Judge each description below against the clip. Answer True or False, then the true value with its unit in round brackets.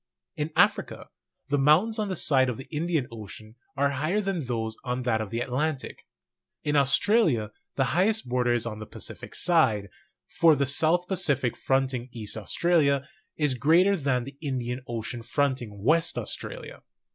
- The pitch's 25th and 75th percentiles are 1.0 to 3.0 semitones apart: False (5.0 semitones)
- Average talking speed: True (165 wpm)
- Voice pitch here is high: False (135 Hz)